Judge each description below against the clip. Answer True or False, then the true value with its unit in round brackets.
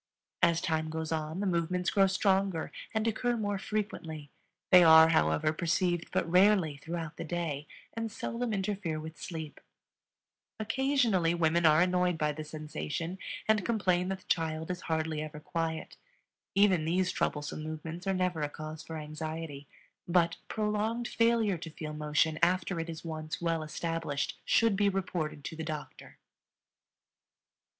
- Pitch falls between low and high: True (165 Hz)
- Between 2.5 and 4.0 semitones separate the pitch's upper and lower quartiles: True (3.5 semitones)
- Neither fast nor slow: True (150 wpm)